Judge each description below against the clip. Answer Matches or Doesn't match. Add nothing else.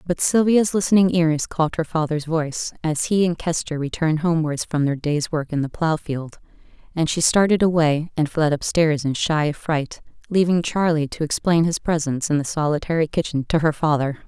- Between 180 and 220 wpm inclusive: Matches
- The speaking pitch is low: Doesn't match